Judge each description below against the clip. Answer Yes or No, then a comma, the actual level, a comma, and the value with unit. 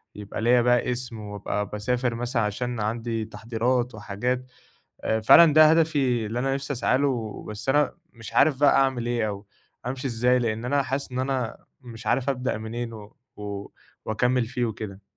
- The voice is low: Yes, low, 120 Hz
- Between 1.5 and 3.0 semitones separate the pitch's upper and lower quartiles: Yes, average, 2.7 semitones